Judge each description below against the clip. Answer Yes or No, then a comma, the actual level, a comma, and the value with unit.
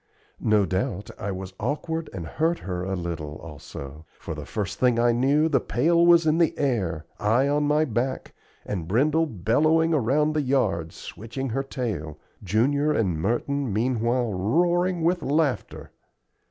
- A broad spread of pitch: Yes, wide, 7.7 semitones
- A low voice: Yes, low, 120 Hz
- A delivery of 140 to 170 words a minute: Yes, average, 155 wpm